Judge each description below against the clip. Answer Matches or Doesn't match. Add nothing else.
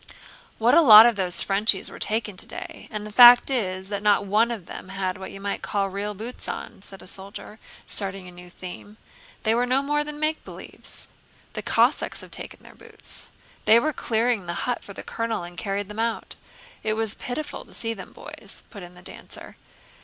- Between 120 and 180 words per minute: Doesn't match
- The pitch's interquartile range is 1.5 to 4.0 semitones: Matches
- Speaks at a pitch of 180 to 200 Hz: Doesn't match